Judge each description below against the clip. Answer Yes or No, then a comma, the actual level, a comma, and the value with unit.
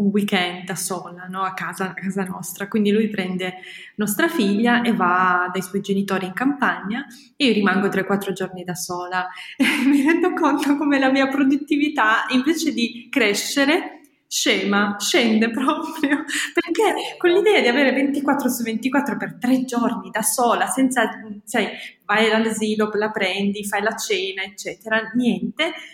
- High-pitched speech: Yes, high, 225 Hz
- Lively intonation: Yes, wide, 5.9 semitones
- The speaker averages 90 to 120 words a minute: No, average, 155 wpm